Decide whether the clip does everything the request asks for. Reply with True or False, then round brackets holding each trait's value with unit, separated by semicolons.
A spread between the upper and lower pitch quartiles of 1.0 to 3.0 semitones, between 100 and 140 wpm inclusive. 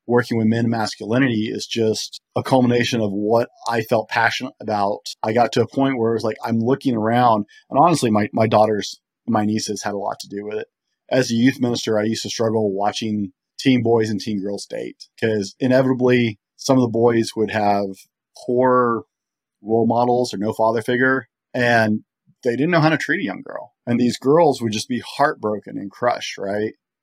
False (2.5 semitones; 205 wpm)